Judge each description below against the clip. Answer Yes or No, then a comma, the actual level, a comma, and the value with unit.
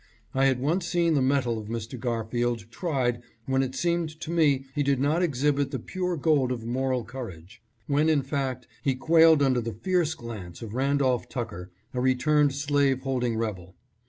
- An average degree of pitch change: Yes, average, 3.6 semitones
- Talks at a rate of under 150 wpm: No, average, 185 wpm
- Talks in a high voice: No, low, 130 Hz